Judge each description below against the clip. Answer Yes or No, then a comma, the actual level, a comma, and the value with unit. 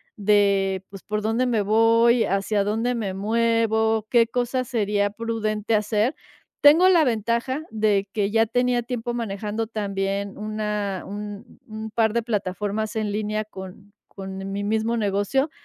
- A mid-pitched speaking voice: No, high, 215 Hz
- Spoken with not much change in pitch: Yes, narrow, 2.2 semitones